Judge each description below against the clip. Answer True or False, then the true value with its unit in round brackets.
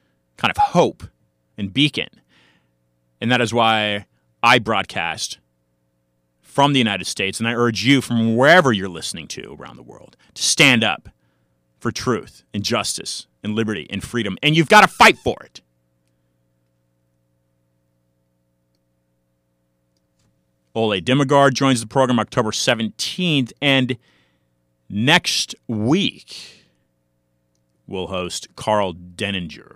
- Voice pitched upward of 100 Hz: False (80 Hz)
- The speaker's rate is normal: False (120 wpm)